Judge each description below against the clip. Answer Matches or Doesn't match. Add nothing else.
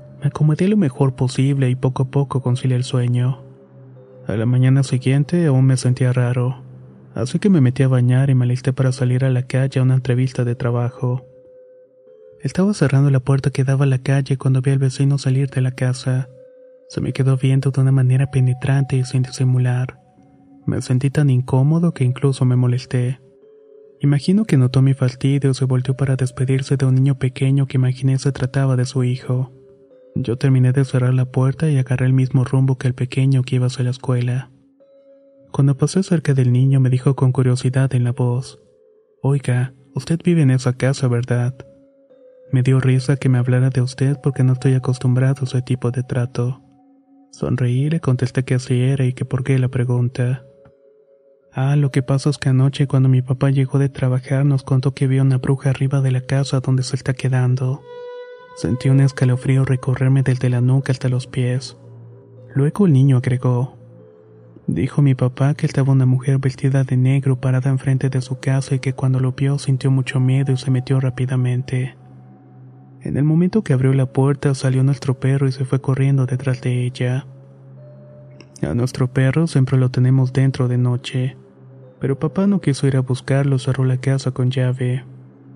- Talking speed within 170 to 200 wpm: Matches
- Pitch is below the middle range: Matches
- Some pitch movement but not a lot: Doesn't match